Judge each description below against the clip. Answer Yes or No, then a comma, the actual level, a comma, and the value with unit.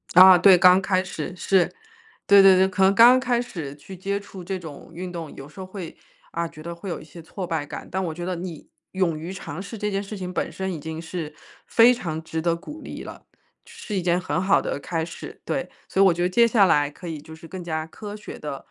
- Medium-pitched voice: Yes, medium, 180 Hz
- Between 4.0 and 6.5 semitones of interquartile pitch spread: No, average, 3.0 semitones